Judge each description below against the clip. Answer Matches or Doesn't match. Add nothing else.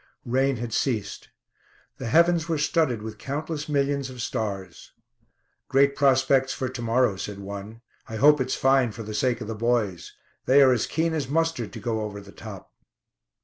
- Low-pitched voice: Matches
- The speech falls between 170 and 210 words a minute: Matches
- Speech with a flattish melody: Doesn't match